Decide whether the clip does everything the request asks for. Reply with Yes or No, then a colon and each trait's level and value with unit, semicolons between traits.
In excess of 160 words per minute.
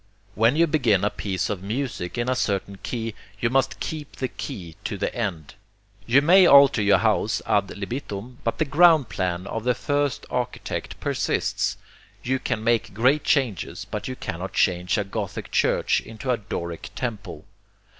Yes: average, 170 wpm